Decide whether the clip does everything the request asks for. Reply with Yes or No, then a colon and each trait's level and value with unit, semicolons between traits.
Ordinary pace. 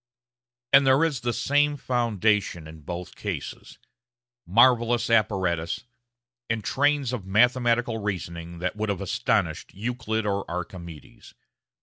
No: slow, 115 wpm